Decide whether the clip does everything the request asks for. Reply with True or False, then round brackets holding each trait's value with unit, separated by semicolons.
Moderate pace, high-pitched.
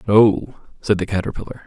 False (145 wpm; 105 Hz)